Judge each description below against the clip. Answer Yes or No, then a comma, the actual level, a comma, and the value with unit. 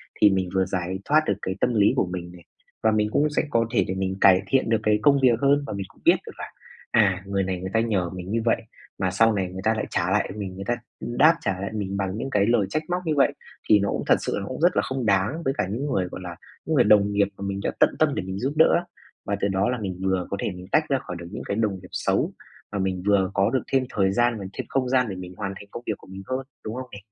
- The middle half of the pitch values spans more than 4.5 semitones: No, average, 4.2 semitones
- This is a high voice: No, low, 100 Hz